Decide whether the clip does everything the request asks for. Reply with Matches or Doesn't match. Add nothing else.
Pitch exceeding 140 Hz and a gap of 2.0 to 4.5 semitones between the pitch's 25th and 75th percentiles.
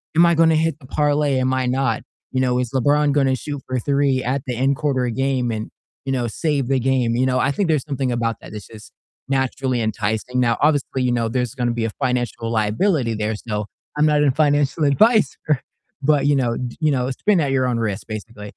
Doesn't match